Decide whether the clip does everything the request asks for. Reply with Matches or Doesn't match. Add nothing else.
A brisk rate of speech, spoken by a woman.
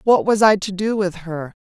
Matches